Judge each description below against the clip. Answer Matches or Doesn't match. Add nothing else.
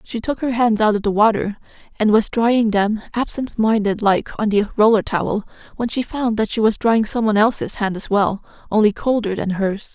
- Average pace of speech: Doesn't match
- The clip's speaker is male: Doesn't match